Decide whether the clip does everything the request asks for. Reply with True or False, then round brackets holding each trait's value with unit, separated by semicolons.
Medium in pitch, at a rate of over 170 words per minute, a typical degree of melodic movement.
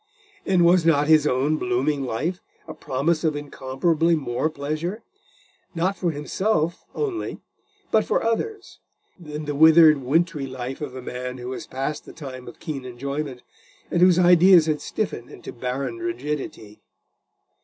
False (150 Hz; 150 wpm; 4.4 semitones)